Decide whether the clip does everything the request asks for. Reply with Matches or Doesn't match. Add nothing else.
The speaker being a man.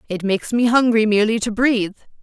Doesn't match